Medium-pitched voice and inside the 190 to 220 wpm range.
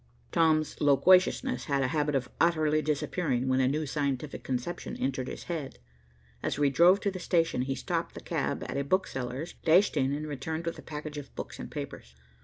Yes: medium, 150 Hz; average, 195 wpm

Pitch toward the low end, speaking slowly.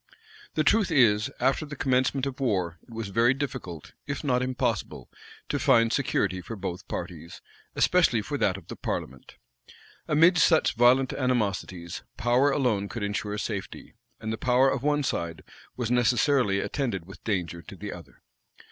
No: low, 120 Hz; average, 165 wpm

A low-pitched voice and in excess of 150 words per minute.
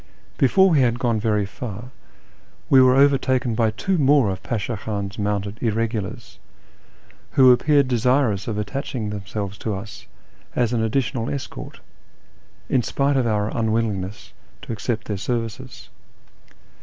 No: low, 115 Hz; slow, 135 wpm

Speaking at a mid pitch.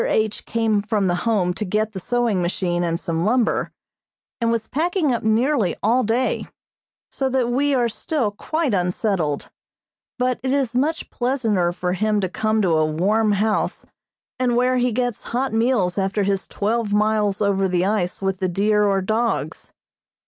No: high, 215 Hz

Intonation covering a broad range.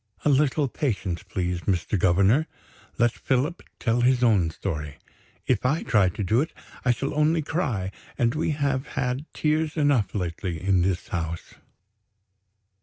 Yes: wide, 7.4 semitones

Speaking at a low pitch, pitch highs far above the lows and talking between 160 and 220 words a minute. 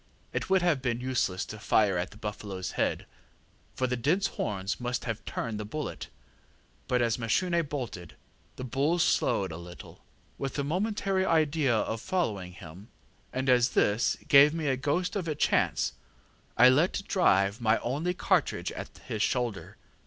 Yes: low, 125 Hz; wide, 6.4 semitones; average, 165 wpm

